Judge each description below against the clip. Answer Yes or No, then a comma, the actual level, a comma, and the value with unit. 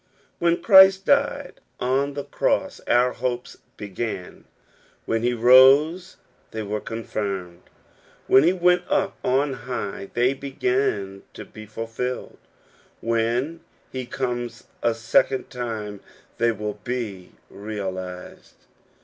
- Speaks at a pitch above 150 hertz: No, low, 120 Hz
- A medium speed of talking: No, slow, 115 wpm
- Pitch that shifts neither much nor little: Yes, average, 4.2 semitones